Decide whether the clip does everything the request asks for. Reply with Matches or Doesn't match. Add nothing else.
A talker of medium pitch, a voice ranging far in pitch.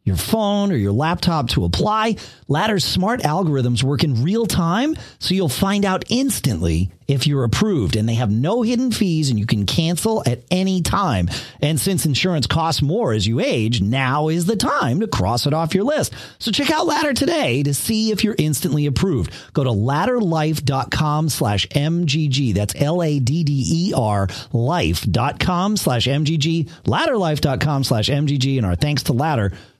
Matches